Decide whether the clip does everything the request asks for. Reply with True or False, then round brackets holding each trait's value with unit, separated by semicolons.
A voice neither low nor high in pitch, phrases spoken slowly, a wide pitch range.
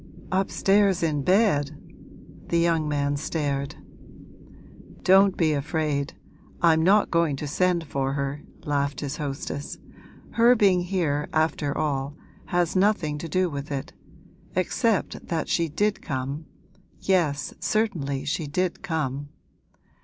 False (155 Hz; 125 wpm; 4.3 semitones)